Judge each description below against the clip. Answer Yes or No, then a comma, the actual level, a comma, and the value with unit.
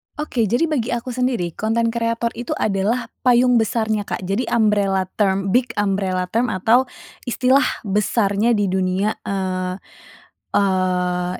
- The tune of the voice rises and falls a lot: No, average, 3.8 semitones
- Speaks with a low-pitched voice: No, high, 210 Hz